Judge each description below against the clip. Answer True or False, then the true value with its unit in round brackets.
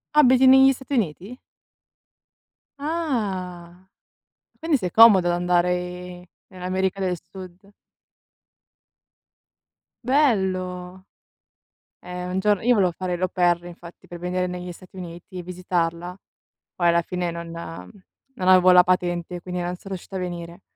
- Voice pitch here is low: False (180 Hz)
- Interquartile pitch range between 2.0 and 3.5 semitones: False (1.6 semitones)